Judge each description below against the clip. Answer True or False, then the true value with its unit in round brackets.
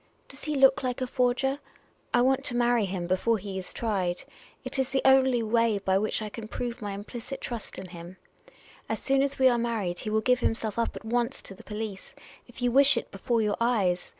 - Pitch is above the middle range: True (230 Hz)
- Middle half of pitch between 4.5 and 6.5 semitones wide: False (4.0 semitones)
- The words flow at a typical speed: False (230 wpm)